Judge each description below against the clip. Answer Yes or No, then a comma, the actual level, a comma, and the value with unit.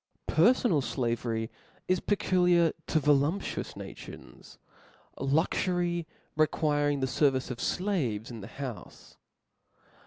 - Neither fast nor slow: No, slow, 105 wpm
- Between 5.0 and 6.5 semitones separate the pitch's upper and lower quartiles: Yes, average, 5.3 semitones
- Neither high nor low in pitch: Yes, medium, 150 Hz